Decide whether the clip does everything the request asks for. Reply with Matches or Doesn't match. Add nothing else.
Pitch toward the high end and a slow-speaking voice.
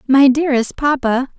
Matches